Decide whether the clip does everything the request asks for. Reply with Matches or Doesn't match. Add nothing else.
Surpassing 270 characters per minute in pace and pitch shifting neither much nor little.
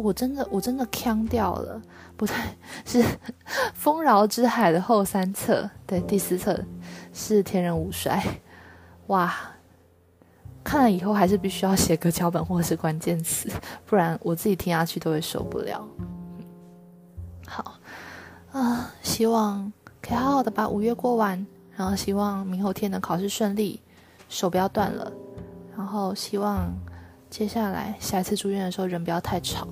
Doesn't match